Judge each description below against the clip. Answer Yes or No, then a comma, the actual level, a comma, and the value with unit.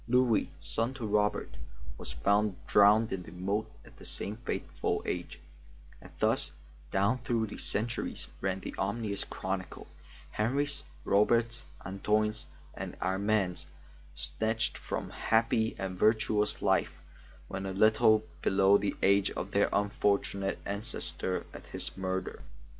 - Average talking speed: No, slow, 130 wpm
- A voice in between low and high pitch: No, low, 105 Hz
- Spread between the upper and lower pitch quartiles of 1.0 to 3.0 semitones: Yes, narrow, 2.5 semitones